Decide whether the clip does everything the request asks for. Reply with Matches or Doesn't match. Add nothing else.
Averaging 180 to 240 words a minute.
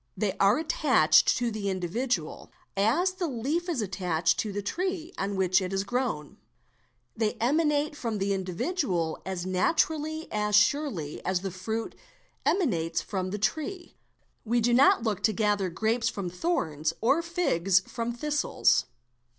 Doesn't match